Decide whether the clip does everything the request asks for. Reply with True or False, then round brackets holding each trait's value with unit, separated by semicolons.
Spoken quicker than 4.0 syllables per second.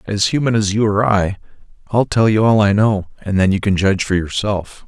True (5.3 syllables/s)